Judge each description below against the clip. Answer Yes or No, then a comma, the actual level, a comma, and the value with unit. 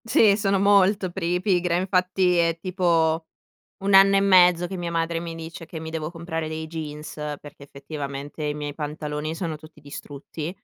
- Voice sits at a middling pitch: Yes, medium, 165 Hz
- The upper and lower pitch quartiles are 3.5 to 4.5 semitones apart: No, average, 2.9 semitones